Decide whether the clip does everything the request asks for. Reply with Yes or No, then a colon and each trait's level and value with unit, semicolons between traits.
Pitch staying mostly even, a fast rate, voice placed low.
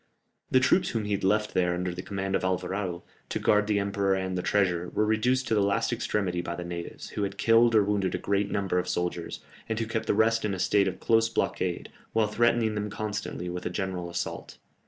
No: average, 3.0 semitones; fast, 230 wpm; low, 100 Hz